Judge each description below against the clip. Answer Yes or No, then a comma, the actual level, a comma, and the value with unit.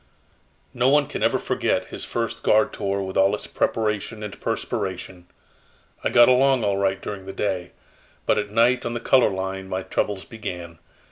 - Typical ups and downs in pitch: Yes, average, 3.5 semitones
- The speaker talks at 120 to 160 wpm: No, average, 180 wpm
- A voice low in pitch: Yes, low, 105 Hz